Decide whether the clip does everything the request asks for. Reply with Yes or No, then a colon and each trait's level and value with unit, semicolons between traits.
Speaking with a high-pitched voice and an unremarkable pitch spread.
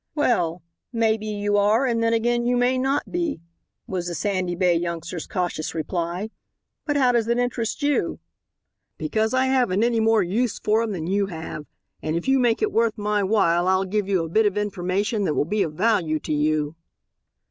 Yes: high, 205 Hz; average, 4.9 semitones